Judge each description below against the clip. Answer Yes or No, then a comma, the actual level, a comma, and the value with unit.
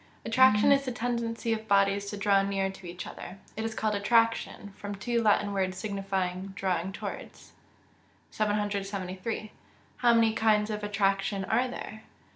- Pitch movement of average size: No, narrow, 2.3 semitones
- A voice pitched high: Yes, high, 205 Hz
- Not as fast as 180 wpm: Yes, average, 155 wpm